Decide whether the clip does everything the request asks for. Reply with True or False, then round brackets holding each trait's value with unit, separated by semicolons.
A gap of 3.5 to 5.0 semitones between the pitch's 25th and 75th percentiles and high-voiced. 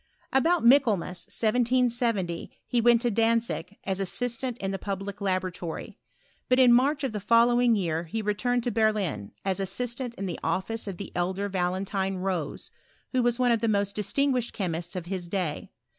True (4.3 semitones; 210 Hz)